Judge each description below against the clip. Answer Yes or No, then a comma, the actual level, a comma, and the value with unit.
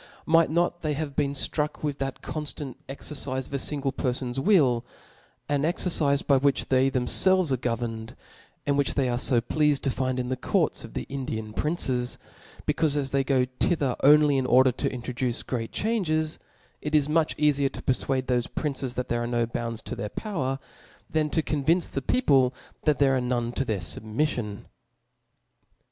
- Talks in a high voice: No, low, 135 Hz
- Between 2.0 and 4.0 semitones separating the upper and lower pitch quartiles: Yes, average, 3.3 semitones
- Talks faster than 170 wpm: Yes, average, 185 wpm